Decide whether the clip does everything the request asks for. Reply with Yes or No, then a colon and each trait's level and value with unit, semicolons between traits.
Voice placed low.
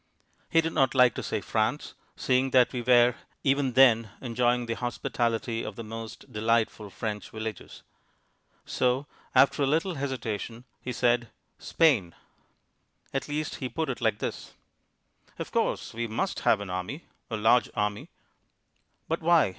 Yes: low, 120 Hz